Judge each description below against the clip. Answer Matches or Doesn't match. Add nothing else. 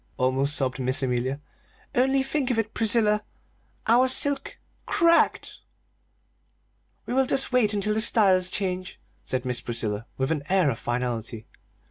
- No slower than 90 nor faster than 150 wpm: Matches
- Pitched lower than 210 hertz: Matches